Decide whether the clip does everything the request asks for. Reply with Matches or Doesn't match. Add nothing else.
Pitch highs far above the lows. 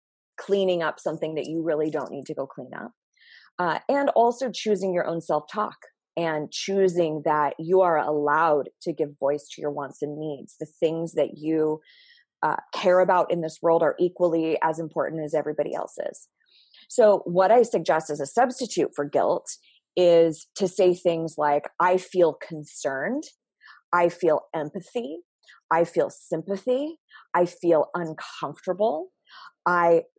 Doesn't match